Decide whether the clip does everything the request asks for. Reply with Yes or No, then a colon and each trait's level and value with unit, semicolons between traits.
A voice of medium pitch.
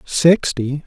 Yes: medium, 145 Hz